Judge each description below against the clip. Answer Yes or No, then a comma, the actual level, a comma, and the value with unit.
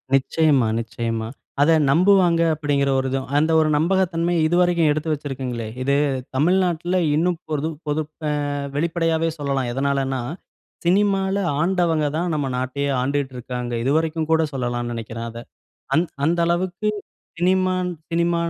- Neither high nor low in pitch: Yes, medium, 155 Hz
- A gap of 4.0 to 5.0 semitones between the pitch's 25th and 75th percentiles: Yes, average, 4.4 semitones